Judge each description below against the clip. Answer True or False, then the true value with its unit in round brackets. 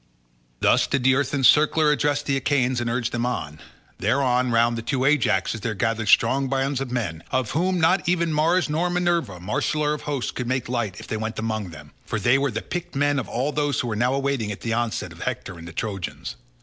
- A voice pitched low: True (130 Hz)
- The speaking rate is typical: False (220 wpm)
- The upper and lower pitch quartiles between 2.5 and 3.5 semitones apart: False (4.4 semitones)